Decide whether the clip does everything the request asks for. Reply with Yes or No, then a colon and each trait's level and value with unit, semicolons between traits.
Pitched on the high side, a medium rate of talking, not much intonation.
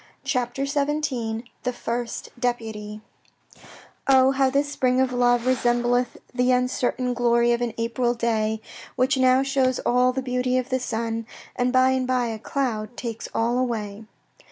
Yes: high, 245 Hz; average, 155 wpm; narrow, 1.7 semitones